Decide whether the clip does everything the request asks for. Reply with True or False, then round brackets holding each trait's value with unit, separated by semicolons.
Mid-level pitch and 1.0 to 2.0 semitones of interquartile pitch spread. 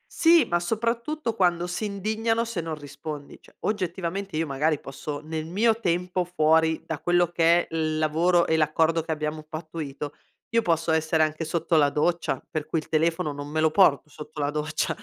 False (165 Hz; 2.6 semitones)